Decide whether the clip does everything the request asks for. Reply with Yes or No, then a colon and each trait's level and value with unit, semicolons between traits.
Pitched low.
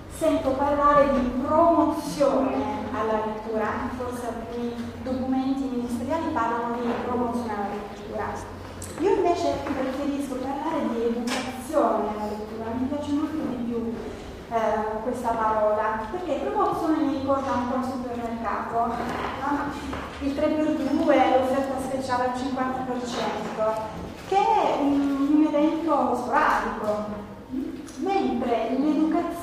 No: very high, 260 Hz